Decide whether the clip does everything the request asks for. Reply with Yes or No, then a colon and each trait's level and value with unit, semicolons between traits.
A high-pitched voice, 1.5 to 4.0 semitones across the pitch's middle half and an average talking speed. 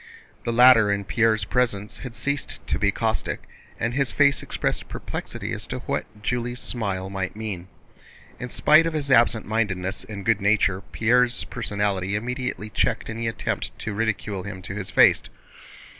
No: low, 110 Hz; average, 3.5 semitones; average, 160 wpm